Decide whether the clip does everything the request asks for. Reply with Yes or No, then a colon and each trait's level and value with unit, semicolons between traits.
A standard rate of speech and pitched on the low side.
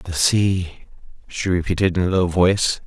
Yes: average, 170 wpm; very low, 90 Hz